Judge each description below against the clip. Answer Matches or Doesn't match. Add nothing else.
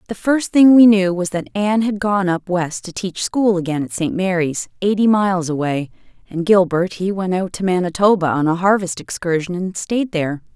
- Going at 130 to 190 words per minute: Doesn't match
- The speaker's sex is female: Matches